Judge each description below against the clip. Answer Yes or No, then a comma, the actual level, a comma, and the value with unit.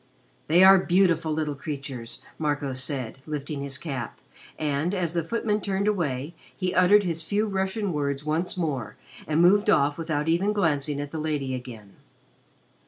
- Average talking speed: Yes, average, 160 wpm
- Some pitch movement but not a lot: Yes, average, 4.5 semitones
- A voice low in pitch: No, medium, 155 Hz